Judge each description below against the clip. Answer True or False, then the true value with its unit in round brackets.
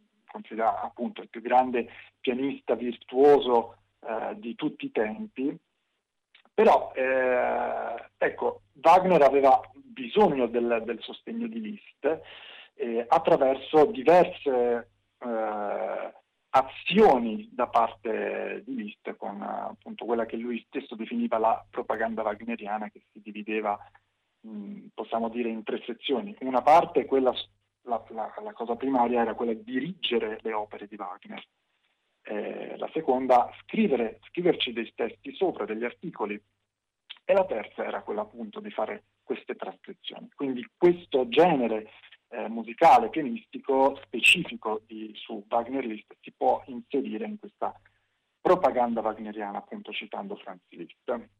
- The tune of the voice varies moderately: False (6.4 semitones)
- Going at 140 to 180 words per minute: False (125 wpm)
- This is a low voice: True (120 Hz)